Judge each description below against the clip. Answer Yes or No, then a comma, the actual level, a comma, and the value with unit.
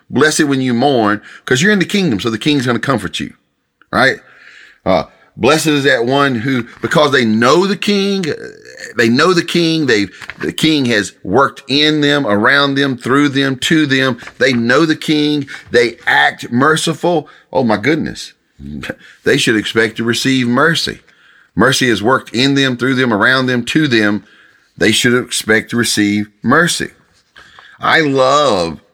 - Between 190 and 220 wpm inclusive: No, average, 165 wpm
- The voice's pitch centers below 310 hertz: Yes, low, 135 Hz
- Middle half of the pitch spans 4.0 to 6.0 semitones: Yes, average, 4.6 semitones